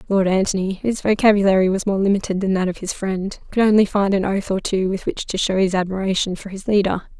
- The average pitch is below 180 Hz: No, high, 195 Hz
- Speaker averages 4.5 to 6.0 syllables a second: No, 6.2 syllables/s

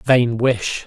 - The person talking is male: Yes, male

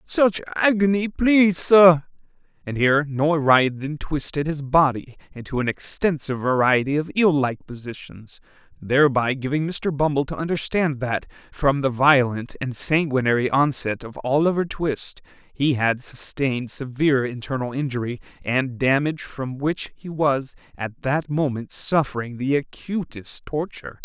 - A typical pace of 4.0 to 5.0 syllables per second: Yes, 4.7 syllables/s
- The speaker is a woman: No, male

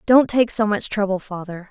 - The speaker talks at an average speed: No, fast, 210 wpm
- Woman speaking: Yes, female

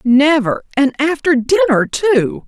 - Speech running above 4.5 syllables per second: No, 3.7 syllables/s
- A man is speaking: No, female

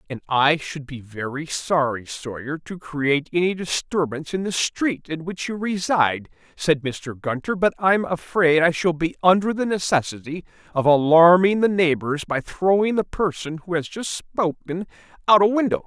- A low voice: No, medium, 165 Hz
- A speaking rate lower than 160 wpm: No, average, 170 wpm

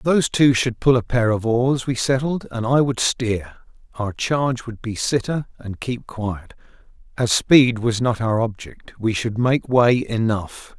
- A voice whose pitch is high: No, low, 120 Hz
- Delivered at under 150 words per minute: No, average, 185 wpm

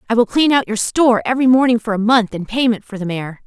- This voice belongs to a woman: Yes, female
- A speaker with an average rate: No, fast, 275 wpm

